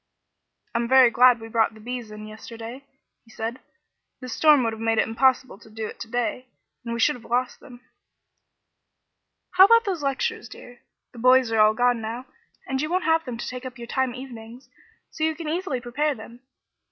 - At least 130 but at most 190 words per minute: No, average, 200 wpm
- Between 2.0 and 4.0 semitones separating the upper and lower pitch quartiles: Yes, average, 2.7 semitones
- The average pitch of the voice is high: Yes, high, 245 Hz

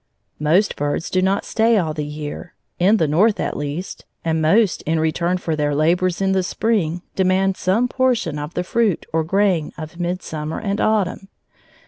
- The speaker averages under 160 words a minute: No, average, 175 wpm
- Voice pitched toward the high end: No, medium, 180 Hz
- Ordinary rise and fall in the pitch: Yes, average, 3.9 semitones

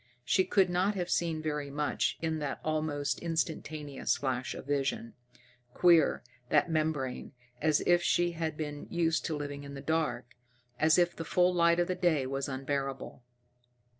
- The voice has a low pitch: No, medium, 155 Hz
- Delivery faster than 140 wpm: Yes, average, 165 wpm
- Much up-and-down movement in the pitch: No, average, 3.1 semitones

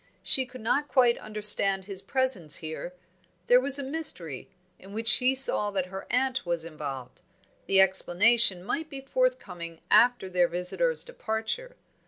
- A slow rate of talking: No, average, 150 wpm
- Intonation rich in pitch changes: Yes, wide, 6.6 semitones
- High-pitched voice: Yes, high, 215 Hz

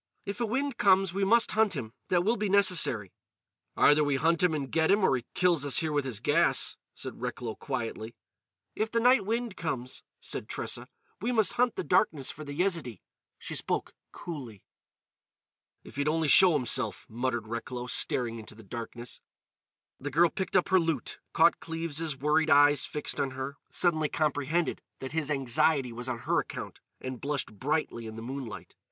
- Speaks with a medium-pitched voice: Yes, medium, 150 Hz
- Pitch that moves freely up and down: Yes, wide, 5.9 semitones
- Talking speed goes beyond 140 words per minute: Yes, average, 180 wpm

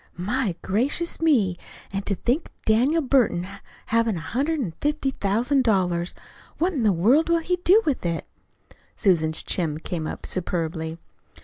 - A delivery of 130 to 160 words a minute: Yes, average, 155 wpm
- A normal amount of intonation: No, wide, 8.3 semitones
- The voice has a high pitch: Yes, high, 220 Hz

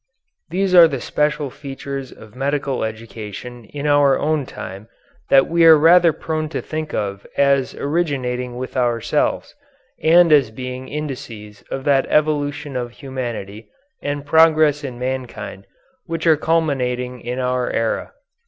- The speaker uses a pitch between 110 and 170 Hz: Yes, low, 135 Hz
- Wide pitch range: No, average, 3.6 semitones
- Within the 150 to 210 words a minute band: No, average, 140 wpm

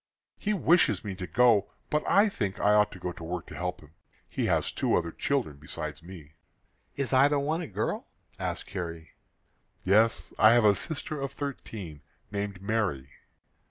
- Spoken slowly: No, average, 175 wpm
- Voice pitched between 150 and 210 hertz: No, low, 105 Hz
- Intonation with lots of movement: Yes, wide, 7.6 semitones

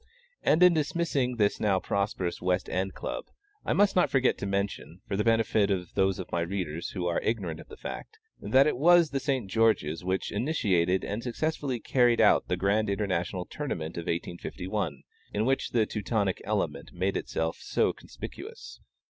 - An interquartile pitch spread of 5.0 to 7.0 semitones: Yes, wide, 5.4 semitones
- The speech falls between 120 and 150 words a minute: No, average, 175 wpm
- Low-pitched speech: Yes, low, 100 Hz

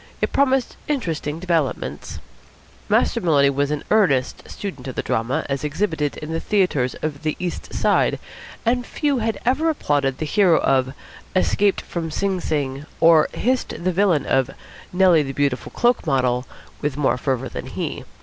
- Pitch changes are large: Yes, wide, 6.0 semitones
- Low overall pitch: No, medium, 155 Hz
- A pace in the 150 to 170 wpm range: Yes, average, 160 wpm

